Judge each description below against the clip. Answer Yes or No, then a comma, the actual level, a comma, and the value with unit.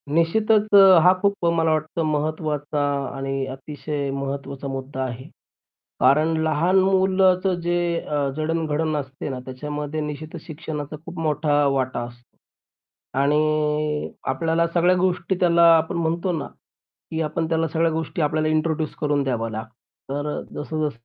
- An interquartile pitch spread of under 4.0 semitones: Yes, narrow, 2.5 semitones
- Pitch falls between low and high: Yes, medium, 155 Hz